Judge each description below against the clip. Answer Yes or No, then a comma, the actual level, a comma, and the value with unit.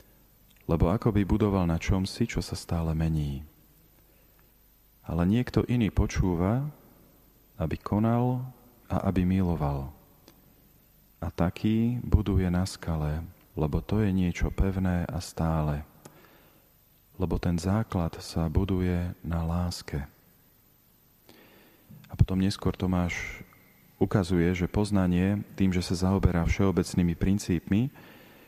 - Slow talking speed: Yes, slow, 105 wpm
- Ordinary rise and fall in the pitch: Yes, average, 3.3 semitones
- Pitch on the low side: Yes, very low, 90 Hz